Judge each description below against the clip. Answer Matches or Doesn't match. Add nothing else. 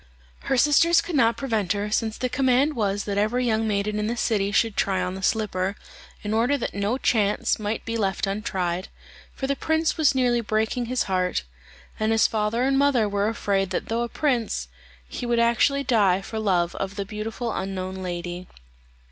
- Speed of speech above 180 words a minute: Matches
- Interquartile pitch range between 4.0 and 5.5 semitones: Doesn't match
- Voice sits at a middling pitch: Doesn't match